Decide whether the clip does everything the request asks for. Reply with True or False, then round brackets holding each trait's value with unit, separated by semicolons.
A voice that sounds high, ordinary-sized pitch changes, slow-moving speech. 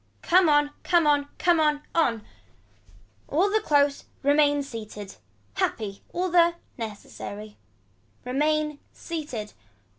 False (290 Hz; 6.1 semitones; 110 wpm)